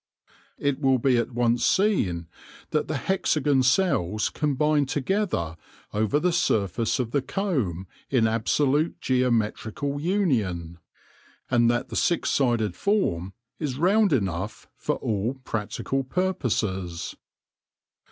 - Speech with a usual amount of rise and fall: No, wide, 6.1 semitones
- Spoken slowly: Yes, slow, 115 wpm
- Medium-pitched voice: No, low, 130 Hz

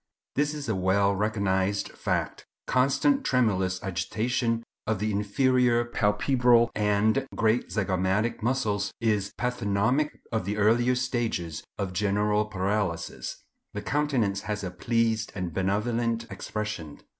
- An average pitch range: Yes, average, 3.1 semitones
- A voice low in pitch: Yes, low, 105 Hz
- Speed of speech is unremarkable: No, slow, 120 wpm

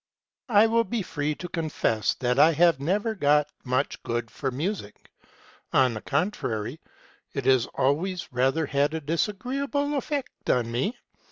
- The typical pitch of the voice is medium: Yes, medium, 155 Hz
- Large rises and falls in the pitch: Yes, wide, 7.7 semitones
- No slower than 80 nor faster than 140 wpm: No, average, 150 wpm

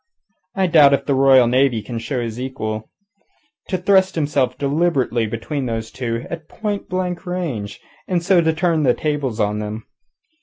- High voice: No, medium, 140 Hz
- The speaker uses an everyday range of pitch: No, wide, 6.6 semitones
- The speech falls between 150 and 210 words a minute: Yes, average, 160 wpm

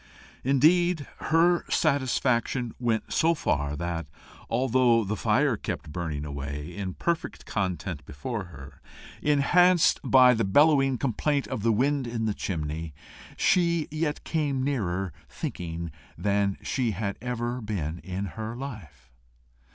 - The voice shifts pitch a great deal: Yes, wide, 7.9 semitones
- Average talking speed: No, slow, 130 wpm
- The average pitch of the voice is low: Yes, low, 115 Hz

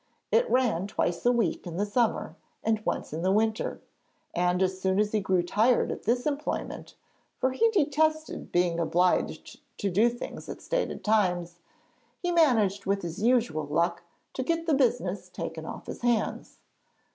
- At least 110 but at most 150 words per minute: No, average, 170 wpm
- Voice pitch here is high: Yes, high, 215 Hz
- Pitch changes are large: Yes, wide, 5.9 semitones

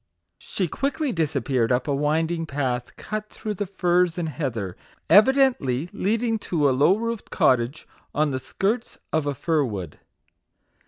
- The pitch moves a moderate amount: No, wide, 7.3 semitones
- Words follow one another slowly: No, average, 150 wpm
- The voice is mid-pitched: Yes, medium, 160 Hz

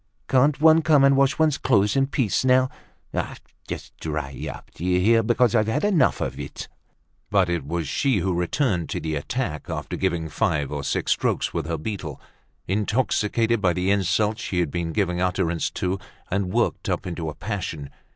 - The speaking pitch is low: Yes, very low, 95 Hz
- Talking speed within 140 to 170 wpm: No, average, 180 wpm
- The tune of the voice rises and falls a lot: Yes, wide, 6.6 semitones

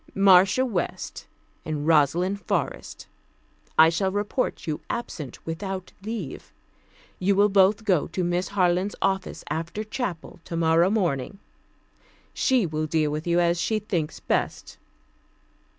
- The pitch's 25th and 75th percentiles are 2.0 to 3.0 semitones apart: No, average, 3.7 semitones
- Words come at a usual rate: No, slow, 125 wpm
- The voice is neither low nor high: Yes, medium, 180 Hz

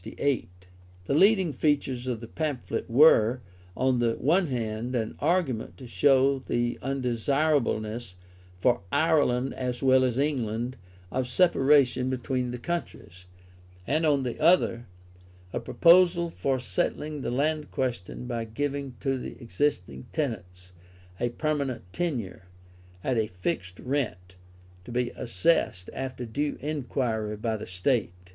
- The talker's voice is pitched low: Yes, low, 130 Hz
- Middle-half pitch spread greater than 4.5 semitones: No, average, 3.9 semitones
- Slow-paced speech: Yes, slow, 130 wpm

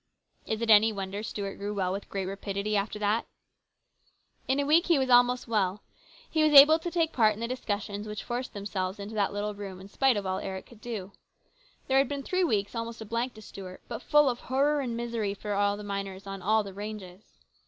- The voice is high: Yes, high, 215 Hz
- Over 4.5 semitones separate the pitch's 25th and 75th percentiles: No, average, 3.7 semitones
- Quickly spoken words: Yes, fast, 220 wpm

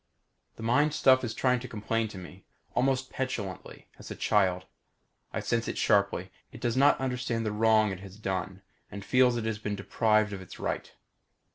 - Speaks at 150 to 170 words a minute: No, average, 185 wpm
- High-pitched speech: No, low, 110 Hz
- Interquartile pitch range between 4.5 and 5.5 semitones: No, average, 3.9 semitones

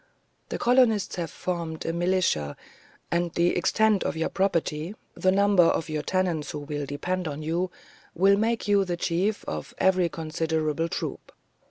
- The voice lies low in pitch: No, medium, 175 Hz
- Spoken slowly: No, average, 165 wpm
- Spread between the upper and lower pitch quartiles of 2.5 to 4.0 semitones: Yes, average, 3.1 semitones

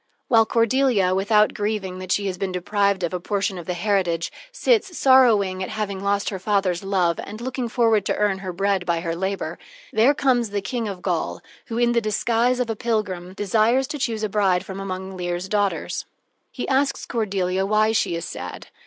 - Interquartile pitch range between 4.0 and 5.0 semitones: No, average, 3.4 semitones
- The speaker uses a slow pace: No, average, 195 wpm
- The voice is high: Yes, high, 200 Hz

